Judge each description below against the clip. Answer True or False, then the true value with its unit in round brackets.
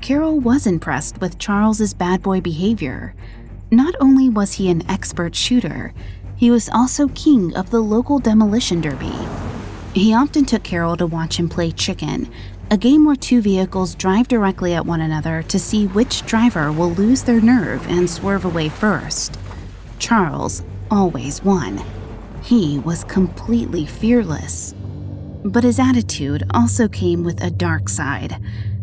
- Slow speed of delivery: False (150 wpm)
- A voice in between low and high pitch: True (175 Hz)